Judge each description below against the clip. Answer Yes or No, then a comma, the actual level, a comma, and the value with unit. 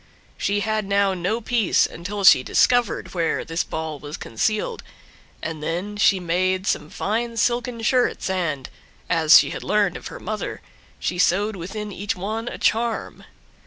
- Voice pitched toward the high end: Yes, high, 200 Hz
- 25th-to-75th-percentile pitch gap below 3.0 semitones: No, average, 4.1 semitones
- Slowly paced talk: No, average, 160 wpm